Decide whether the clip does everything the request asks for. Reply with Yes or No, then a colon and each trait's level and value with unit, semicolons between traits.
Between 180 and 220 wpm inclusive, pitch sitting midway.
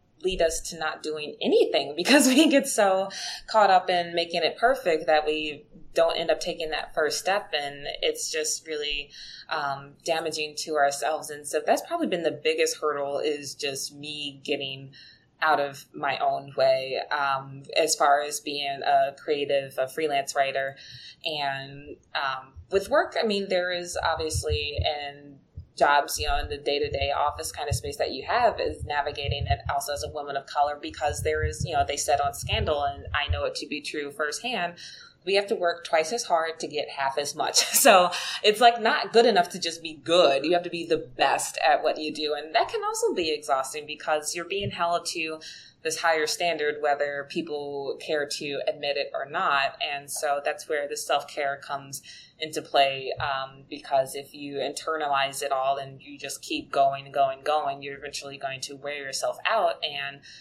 Yes: average, 200 wpm; medium, 150 Hz